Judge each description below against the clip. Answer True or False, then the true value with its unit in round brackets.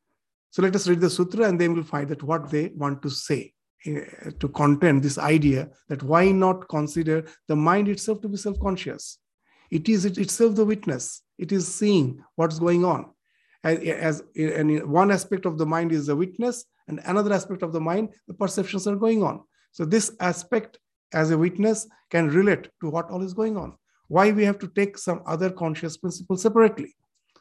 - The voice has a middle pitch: True (180 Hz)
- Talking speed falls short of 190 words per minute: False (195 wpm)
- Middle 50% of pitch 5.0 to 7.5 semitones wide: False (4.0 semitones)